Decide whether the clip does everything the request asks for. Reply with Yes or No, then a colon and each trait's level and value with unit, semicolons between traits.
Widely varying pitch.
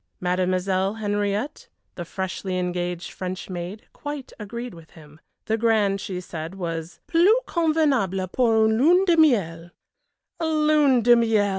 Yes: wide, 5.7 semitones